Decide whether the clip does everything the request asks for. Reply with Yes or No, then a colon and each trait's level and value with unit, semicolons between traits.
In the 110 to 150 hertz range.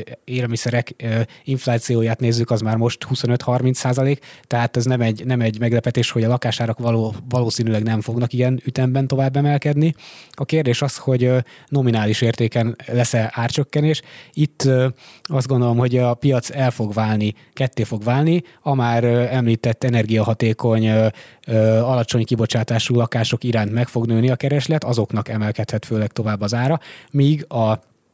Yes: low, 120 Hz